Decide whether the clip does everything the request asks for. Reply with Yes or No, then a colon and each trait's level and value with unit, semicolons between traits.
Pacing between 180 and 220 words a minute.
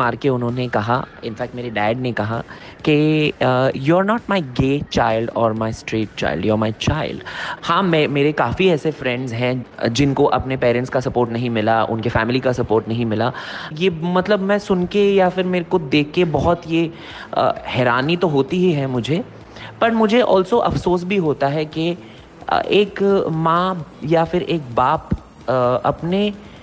Yes: average, 185 wpm